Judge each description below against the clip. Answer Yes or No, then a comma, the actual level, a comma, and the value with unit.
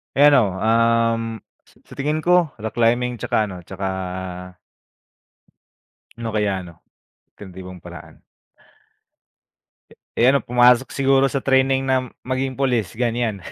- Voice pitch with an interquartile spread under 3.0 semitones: No, average, 3.7 semitones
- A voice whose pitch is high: No, low, 120 Hz